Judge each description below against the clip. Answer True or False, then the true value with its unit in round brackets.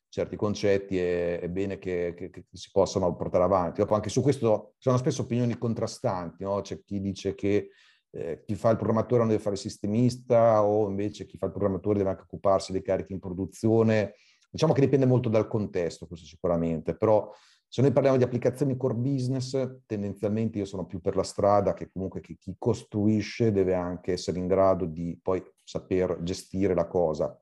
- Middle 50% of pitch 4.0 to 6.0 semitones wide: False (3.3 semitones)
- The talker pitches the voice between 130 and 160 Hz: False (100 Hz)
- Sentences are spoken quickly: True (190 wpm)